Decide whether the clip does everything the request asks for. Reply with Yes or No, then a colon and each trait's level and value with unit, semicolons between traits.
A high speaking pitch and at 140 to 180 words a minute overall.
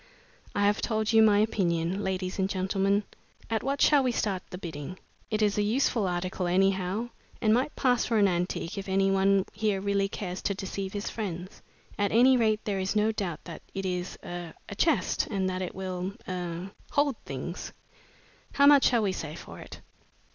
No: high, 195 Hz; average, 190 wpm